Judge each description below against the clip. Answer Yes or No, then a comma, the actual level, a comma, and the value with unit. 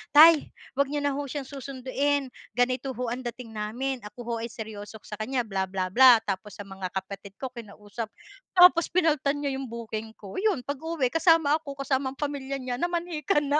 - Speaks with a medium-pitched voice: No, very high, 260 Hz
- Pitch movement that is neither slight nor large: Yes, average, 4.6 semitones